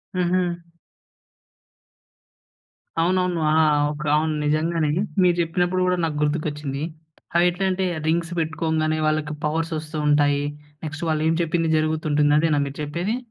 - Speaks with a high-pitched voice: No, medium, 160 Hz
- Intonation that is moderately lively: No, narrow, 2.2 semitones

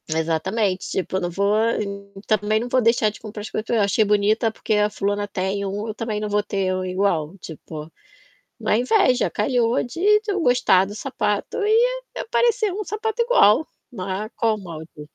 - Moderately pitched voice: No, high, 210 Hz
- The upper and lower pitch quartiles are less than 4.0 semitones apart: No, average, 4.3 semitones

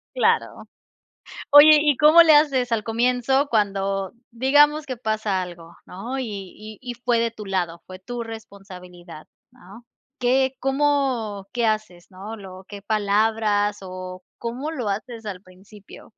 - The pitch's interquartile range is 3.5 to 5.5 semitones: Yes, average, 4.5 semitones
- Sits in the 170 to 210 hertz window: No, high, 220 Hz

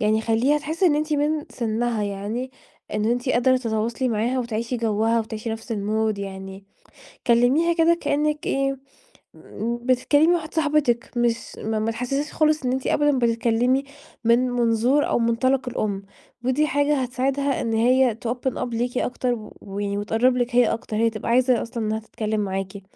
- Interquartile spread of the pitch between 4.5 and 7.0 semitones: No, average, 3.3 semitones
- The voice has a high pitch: Yes, high, 240 Hz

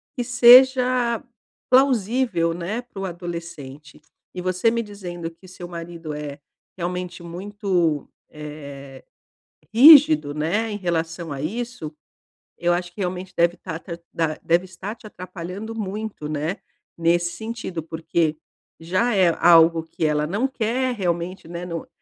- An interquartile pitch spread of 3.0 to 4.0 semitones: No, average, 4.8 semitones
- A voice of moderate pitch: Yes, medium, 175 Hz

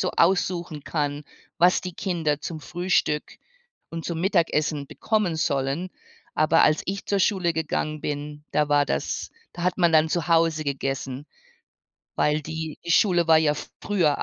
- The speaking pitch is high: No, medium, 160 Hz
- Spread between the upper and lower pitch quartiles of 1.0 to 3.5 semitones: Yes, average, 2.8 semitones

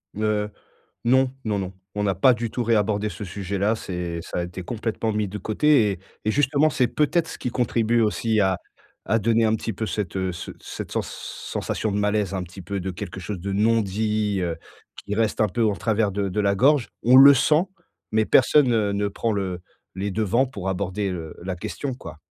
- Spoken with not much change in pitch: No, average, 3.0 semitones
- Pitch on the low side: Yes, low, 105 Hz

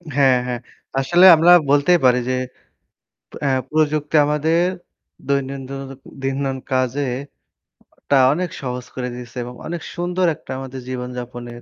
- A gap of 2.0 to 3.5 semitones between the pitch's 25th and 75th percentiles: Yes, average, 3.1 semitones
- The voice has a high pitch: No, low, 135 Hz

